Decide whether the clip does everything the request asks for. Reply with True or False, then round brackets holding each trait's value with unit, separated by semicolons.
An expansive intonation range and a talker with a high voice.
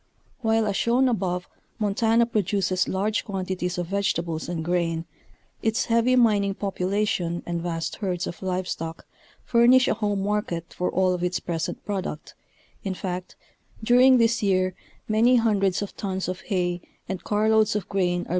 False (3.4 semitones; 195 Hz)